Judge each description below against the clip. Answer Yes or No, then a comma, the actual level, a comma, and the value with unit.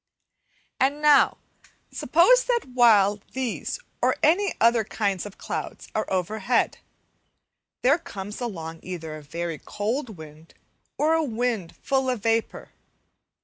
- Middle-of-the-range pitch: No, high, 225 Hz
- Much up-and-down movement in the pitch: Yes, wide, 6.0 semitones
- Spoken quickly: No, slow, 135 wpm